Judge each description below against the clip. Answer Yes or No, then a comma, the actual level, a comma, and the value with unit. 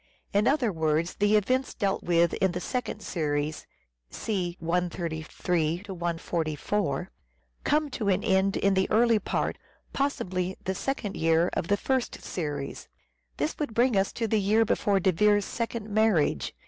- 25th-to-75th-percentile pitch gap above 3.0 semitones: Yes, average, 4.3 semitones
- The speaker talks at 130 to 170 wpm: Yes, average, 150 wpm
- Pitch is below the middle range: No, high, 190 Hz